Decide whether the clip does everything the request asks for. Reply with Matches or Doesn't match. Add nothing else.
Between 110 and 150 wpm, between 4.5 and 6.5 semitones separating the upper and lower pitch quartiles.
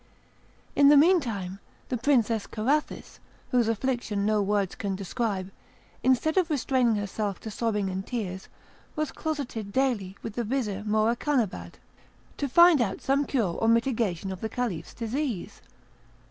Matches